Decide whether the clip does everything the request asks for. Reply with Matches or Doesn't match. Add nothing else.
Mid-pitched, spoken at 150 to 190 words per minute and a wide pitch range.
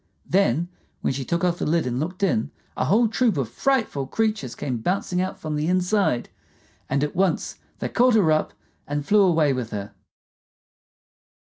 Matches